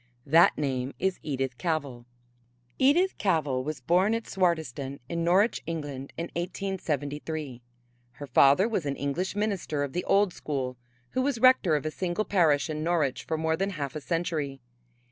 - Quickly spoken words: No, average, 165 wpm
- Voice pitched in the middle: Yes, medium, 160 Hz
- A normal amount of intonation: Yes, average, 4.8 semitones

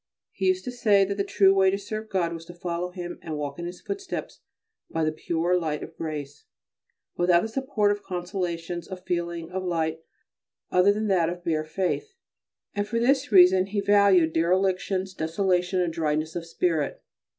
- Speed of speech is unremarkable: Yes, average, 185 wpm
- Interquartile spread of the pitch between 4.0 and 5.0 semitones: No, average, 3.0 semitones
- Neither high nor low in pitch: Yes, medium, 180 Hz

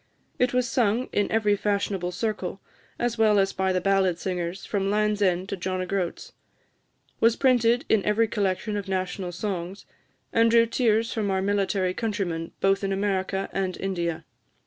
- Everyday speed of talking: Yes, average, 170 wpm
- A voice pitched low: No, high, 200 Hz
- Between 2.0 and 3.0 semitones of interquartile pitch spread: Yes, average, 2.7 semitones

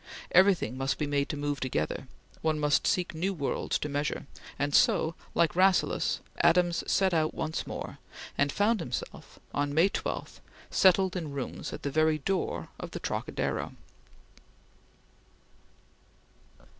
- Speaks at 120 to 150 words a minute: Yes, average, 140 wpm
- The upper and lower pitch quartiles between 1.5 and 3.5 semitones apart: No, average, 3.9 semitones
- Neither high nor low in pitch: Yes, medium, 155 Hz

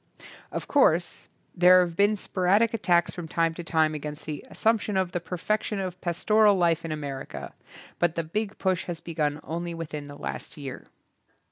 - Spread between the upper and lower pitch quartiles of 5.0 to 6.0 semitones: No, average, 3.1 semitones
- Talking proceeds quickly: No, average, 175 wpm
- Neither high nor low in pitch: Yes, medium, 175 Hz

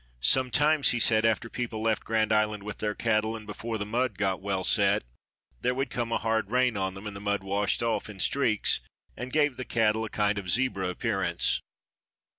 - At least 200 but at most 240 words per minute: Yes, fast, 205 wpm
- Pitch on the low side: Yes, low, 110 Hz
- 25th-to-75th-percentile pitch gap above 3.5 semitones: No, narrow, 2.6 semitones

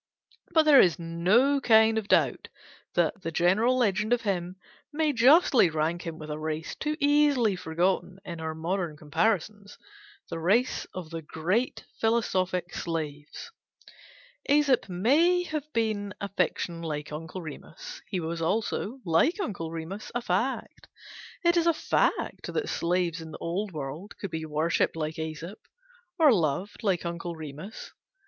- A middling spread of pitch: No, wide, 6.1 semitones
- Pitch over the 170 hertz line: Yes, medium, 185 Hz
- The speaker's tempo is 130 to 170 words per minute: Yes, average, 150 wpm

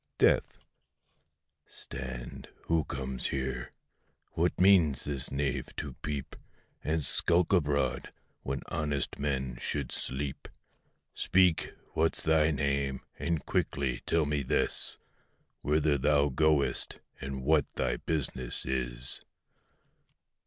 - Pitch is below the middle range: Yes, very low, 70 Hz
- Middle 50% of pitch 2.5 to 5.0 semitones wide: Yes, average, 2.8 semitones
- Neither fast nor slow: No, slow, 105 wpm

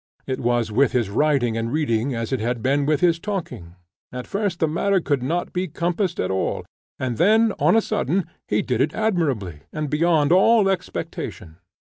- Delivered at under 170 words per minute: No, average, 185 wpm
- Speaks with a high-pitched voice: No, medium, 150 Hz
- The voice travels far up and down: Yes, wide, 6.8 semitones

